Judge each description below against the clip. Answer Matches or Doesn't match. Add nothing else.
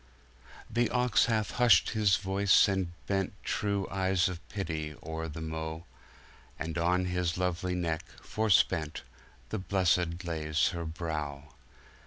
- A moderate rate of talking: Doesn't match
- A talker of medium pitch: Doesn't match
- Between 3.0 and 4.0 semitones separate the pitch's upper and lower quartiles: Matches